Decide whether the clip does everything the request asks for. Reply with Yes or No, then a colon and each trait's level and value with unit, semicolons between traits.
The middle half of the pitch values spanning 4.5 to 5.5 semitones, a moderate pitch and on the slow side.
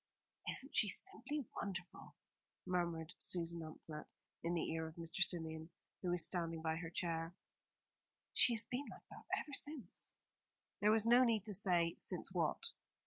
No: average, 5.1 semitones; medium, 175 Hz; average, 155 wpm